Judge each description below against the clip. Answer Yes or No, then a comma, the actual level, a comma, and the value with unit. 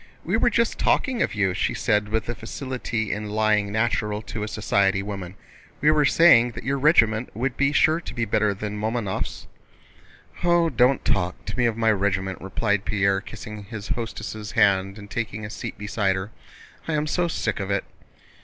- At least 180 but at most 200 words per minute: Yes, average, 190 wpm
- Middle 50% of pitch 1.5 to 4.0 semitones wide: Yes, average, 3.5 semitones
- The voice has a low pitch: Yes, low, 110 Hz